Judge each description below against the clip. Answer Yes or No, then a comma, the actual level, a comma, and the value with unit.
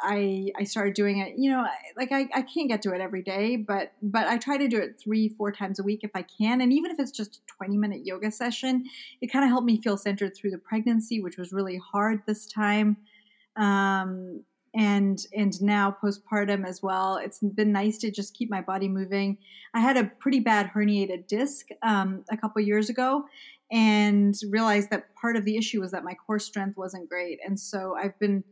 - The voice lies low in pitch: No, high, 210 Hz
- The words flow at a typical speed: No, fast, 220 wpm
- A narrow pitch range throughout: Yes, narrow, 2.3 semitones